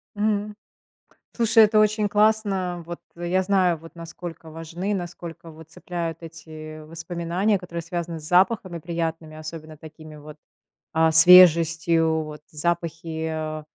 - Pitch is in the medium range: Yes, medium, 170 Hz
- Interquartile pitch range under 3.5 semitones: Yes, narrow, 2.4 semitones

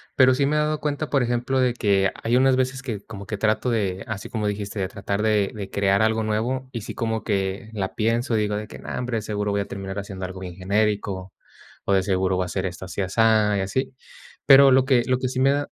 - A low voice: Yes, low, 110 Hz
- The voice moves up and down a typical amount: Yes, average, 4.3 semitones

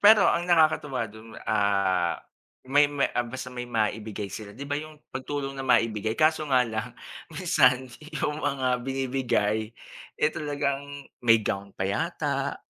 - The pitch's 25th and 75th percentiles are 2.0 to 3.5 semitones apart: No, average, 4.7 semitones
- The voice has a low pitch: Yes, low, 130 Hz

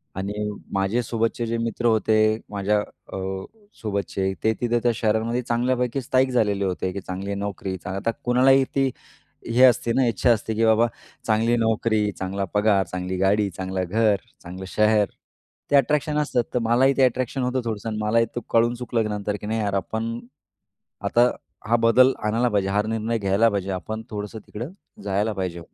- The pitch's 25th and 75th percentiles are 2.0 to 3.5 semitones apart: Yes, average, 3.0 semitones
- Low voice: Yes, low, 110 Hz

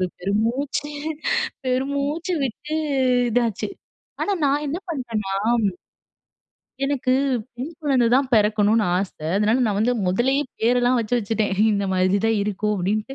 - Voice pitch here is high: Yes, high, 235 Hz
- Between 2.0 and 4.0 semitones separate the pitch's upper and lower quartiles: No, average, 4.5 semitones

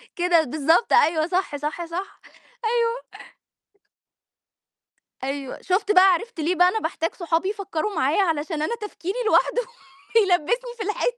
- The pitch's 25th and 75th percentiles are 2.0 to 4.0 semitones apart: No, average, 4.6 semitones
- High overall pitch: Yes, very high, 360 Hz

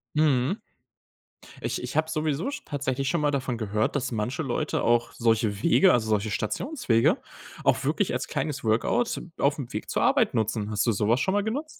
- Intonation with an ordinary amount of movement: No, wide, 5.8 semitones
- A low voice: Yes, low, 130 Hz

